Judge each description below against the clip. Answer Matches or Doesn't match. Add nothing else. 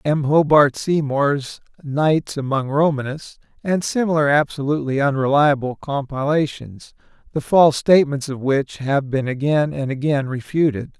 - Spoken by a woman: Doesn't match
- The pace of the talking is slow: Matches